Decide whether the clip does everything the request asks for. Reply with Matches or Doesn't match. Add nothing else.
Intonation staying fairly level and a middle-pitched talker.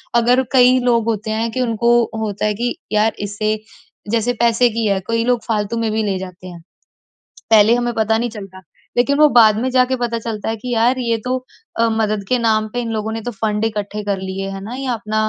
Doesn't match